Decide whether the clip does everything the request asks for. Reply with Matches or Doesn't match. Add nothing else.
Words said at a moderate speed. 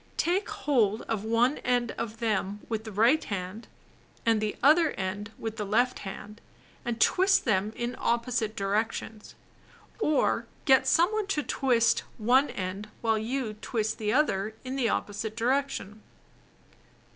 Matches